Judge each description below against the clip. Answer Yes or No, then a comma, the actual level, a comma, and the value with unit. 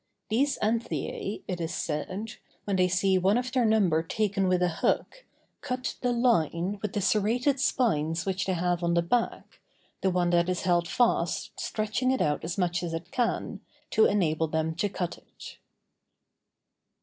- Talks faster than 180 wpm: No, average, 175 wpm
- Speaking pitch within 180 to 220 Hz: Yes, high, 190 Hz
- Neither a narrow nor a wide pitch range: Yes, average, 4.4 semitones